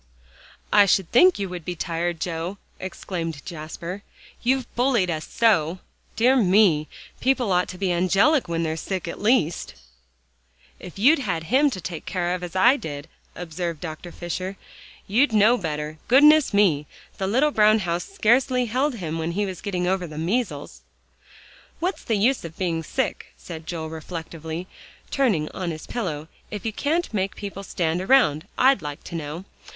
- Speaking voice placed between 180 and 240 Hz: Yes, medium, 185 Hz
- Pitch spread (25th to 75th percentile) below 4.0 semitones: No, wide, 5.6 semitones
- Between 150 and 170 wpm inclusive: Yes, average, 165 wpm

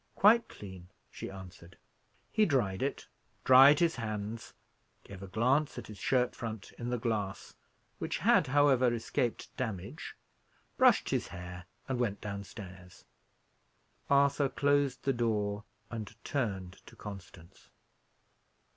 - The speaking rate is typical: No, slow, 125 wpm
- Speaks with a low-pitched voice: Yes, low, 110 Hz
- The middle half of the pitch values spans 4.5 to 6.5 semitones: Yes, average, 5.2 semitones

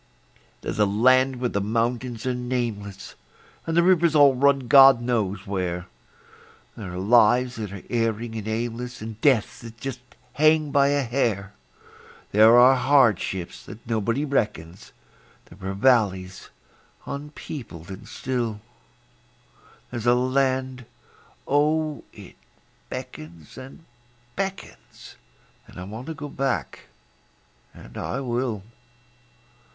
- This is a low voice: Yes, low, 120 Hz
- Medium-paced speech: No, slow, 125 wpm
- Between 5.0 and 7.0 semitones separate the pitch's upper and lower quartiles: No, average, 4.3 semitones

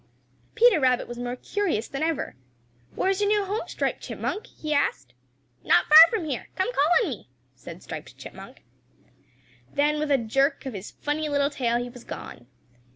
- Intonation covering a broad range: Yes, wide, 6.3 semitones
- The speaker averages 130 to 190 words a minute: Yes, average, 180 wpm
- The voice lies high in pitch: Yes, very high, 290 Hz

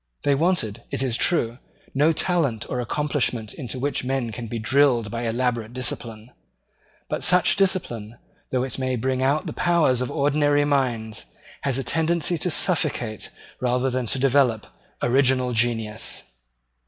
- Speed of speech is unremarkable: Yes, average, 150 wpm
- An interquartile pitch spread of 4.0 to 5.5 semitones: No, average, 3.5 semitones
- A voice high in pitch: No, low, 130 Hz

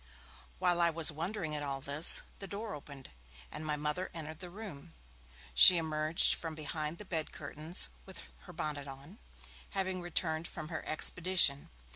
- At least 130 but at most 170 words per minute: Yes, average, 160 wpm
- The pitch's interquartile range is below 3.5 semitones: Yes, average, 3.0 semitones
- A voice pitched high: No, medium, 160 Hz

